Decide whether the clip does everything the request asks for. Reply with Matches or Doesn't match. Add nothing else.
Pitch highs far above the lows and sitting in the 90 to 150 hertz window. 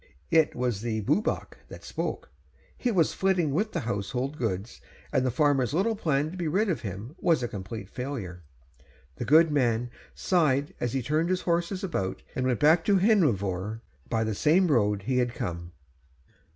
Matches